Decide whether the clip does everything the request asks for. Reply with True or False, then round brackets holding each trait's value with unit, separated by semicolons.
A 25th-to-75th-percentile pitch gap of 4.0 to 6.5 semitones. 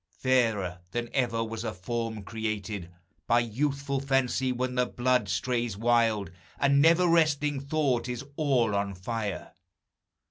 False (3.6 semitones)